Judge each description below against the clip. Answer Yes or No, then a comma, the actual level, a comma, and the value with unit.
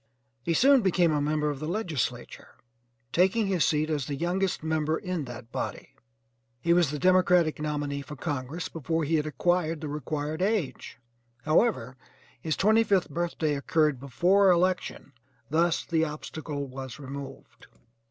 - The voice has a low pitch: No, medium, 155 Hz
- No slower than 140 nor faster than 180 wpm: Yes, average, 150 wpm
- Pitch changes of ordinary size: Yes, average, 3.5 semitones